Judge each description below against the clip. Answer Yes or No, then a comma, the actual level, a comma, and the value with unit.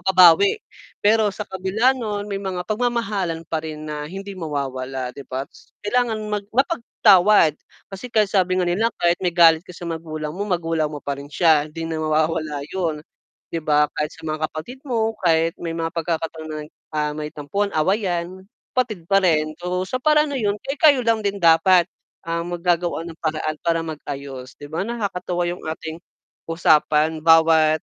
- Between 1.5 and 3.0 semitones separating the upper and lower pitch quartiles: No, average, 4.3 semitones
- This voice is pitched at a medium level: Yes, medium, 170 Hz